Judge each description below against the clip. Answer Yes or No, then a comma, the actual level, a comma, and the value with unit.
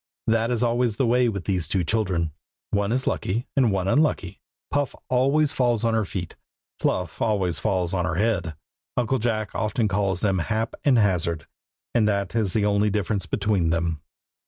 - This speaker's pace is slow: No, average, 180 wpm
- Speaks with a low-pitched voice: Yes, low, 105 Hz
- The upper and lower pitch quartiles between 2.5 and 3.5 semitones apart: No, average, 3.9 semitones